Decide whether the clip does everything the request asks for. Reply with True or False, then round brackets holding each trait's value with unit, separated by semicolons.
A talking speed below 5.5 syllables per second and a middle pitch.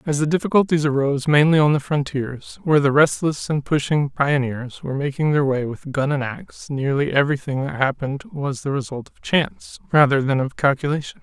False (5.6 syllables/s; 145 Hz)